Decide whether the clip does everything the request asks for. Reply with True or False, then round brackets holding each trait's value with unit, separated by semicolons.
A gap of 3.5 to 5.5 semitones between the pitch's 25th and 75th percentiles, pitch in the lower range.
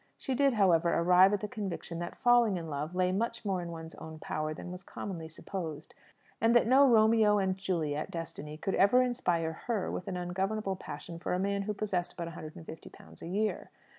False (4.2 semitones; 185 Hz)